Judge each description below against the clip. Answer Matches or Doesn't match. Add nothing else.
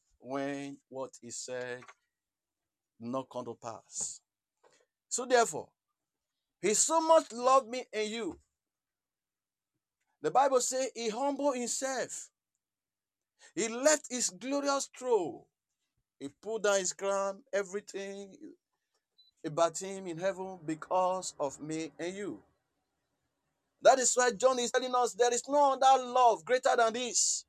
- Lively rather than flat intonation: Matches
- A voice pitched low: Doesn't match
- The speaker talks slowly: Matches